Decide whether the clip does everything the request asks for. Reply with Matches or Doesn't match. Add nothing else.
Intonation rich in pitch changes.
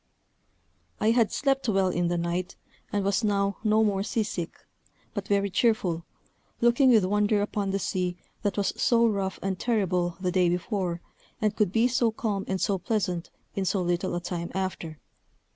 Doesn't match